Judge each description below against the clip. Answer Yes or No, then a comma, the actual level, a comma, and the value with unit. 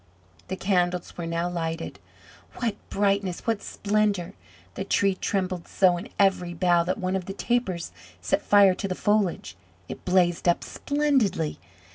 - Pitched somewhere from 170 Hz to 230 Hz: Yes, medium, 185 Hz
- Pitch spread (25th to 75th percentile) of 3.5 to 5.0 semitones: No, narrow, 2.5 semitones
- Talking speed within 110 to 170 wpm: Yes, average, 150 wpm